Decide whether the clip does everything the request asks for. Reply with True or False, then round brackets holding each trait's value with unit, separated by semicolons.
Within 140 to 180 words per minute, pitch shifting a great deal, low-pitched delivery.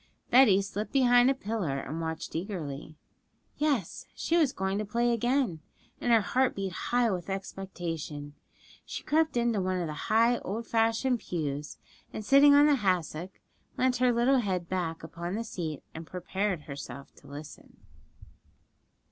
False (155 wpm; 6.5 semitones; 195 Hz)